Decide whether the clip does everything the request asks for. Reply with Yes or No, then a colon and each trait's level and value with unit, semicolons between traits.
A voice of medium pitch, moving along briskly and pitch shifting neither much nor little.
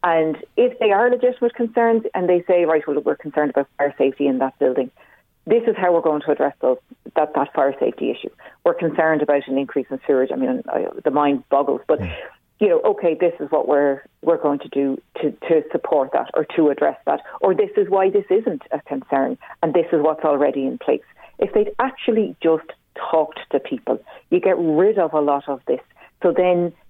No: medium, 160 Hz; fast, 215 wpm; wide, 7.2 semitones